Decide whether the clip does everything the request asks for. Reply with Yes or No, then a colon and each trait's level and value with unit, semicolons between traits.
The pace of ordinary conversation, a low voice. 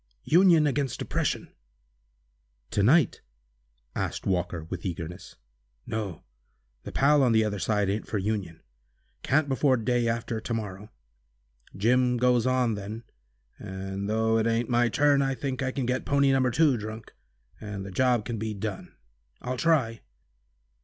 Yes: average, 150 wpm; low, 115 Hz